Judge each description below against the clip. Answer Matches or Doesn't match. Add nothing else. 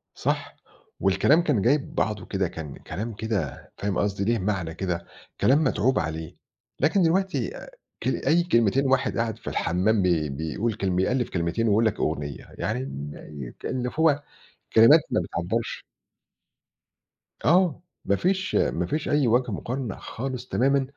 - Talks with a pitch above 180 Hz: Doesn't match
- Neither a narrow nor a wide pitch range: Doesn't match